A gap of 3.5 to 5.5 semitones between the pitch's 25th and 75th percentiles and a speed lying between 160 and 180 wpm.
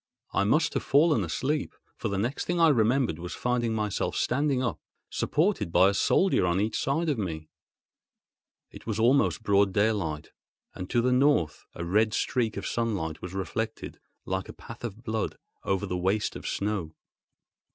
Yes: average, 5.0 semitones; average, 170 wpm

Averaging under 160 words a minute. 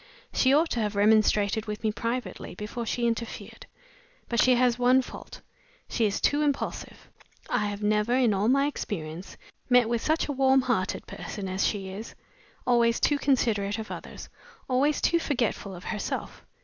No: average, 170 wpm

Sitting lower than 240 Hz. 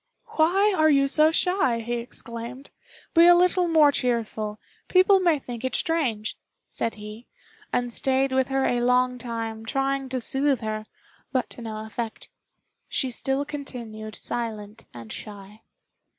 No: very high, 250 Hz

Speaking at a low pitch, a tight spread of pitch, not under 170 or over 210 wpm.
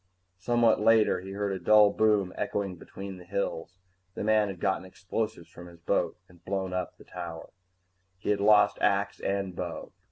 Yes: low, 100 Hz; narrow, 2.3 semitones; average, 180 wpm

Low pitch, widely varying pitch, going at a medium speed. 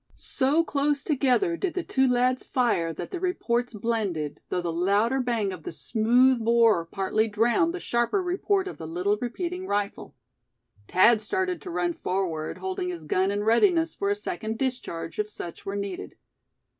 No: high, 235 Hz; wide, 8.6 semitones; average, 170 wpm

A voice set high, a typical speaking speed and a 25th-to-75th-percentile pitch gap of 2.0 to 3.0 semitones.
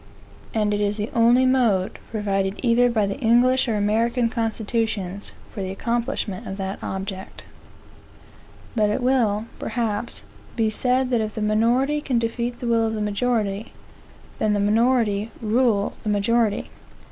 Yes: high, 220 Hz; average, 150 wpm; narrow, 2.5 semitones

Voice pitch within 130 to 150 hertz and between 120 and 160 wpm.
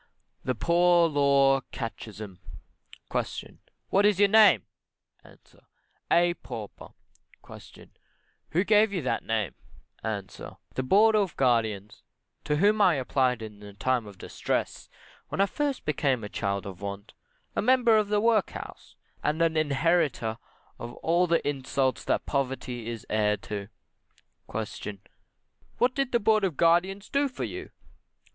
Yes: medium, 140 Hz; average, 140 wpm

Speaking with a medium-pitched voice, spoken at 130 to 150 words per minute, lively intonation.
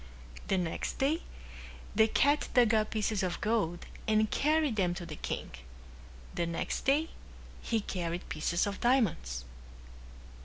No: high, 210 Hz; average, 140 wpm; wide, 5.8 semitones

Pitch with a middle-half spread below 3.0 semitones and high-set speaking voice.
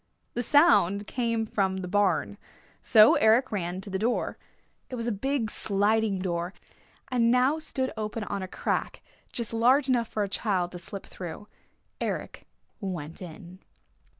No: average, 3.9 semitones; high, 210 Hz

